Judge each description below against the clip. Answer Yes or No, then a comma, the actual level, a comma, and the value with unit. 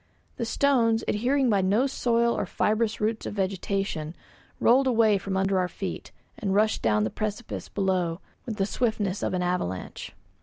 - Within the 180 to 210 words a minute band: No, average, 165 wpm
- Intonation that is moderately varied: Yes, average, 3.5 semitones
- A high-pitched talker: Yes, high, 210 Hz